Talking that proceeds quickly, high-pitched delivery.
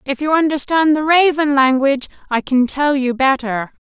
No: average, 170 wpm; very high, 280 Hz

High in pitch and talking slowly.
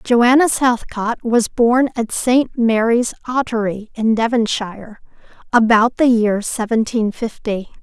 Yes: high, 230 Hz; slow, 115 wpm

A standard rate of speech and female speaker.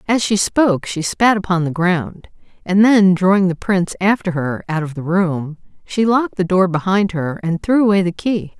No: fast, 210 wpm; female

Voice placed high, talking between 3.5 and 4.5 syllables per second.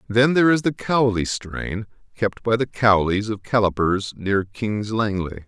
No: low, 110 Hz; 4.4 syllables/s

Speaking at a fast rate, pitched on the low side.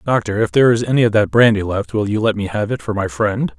Yes: fast, 300 wpm; low, 105 Hz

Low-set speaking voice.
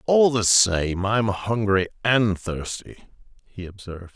Yes: low, 105 Hz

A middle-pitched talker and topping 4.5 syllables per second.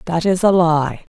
No: medium, 170 Hz; 4.3 syllables/s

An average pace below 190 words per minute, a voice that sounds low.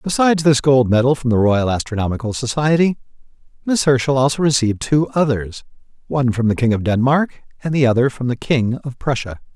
Yes: average, 180 wpm; low, 130 Hz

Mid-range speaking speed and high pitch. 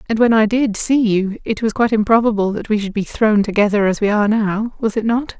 No: fast, 245 wpm; high, 215 Hz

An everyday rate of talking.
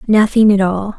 Yes: average, 185 wpm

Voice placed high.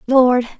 Yes: very high, 250 Hz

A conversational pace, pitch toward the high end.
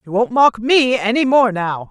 No: fast, 220 wpm; high, 230 Hz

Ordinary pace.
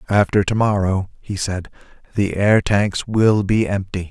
Yes: average, 145 wpm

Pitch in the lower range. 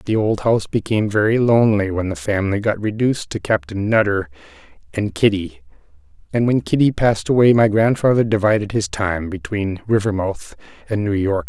Yes: low, 105 Hz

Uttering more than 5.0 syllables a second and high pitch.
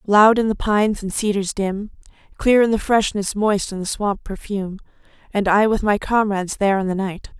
Yes: 5.3 syllables/s; high, 205 Hz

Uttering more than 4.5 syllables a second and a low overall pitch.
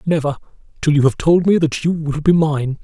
No: 5.3 syllables/s; medium, 155 Hz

